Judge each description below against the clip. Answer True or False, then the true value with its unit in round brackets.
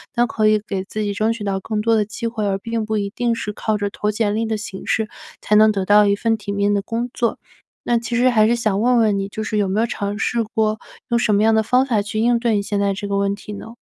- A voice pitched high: True (215 Hz)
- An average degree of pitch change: False (2.0 semitones)